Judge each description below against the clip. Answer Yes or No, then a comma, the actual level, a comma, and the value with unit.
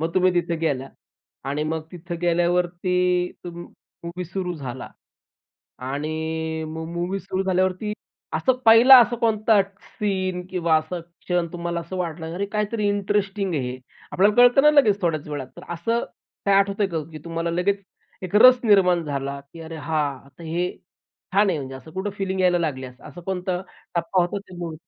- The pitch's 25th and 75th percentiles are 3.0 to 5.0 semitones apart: Yes, average, 3.4 semitones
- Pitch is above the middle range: No, medium, 175 Hz